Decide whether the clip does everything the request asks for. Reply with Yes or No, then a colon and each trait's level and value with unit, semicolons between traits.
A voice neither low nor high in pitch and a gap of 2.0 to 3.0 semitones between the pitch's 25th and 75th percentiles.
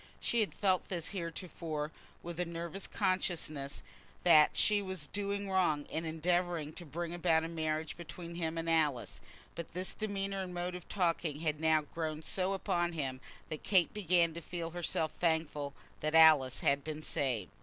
Yes: medium, 165 Hz; narrow, 2.5 semitones